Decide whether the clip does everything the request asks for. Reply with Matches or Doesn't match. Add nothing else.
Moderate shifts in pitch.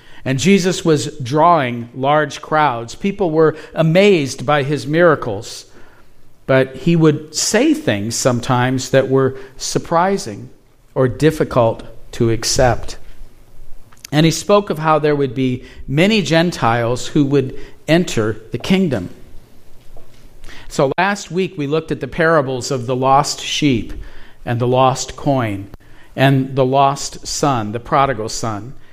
Matches